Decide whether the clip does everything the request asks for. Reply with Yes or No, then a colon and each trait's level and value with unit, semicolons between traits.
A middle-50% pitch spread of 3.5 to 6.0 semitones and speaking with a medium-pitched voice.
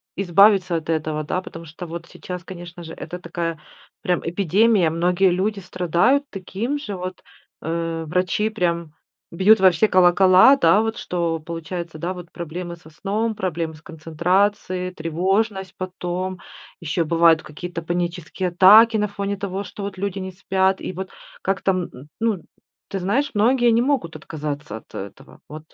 No: average, 2.9 semitones; medium, 180 Hz